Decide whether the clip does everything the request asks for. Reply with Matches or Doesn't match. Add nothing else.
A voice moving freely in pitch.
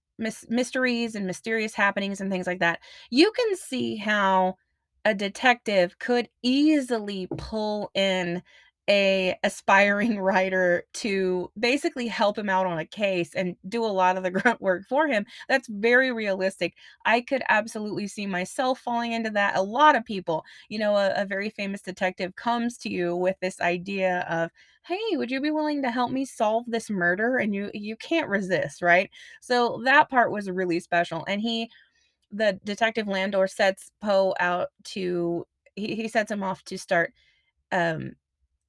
Doesn't match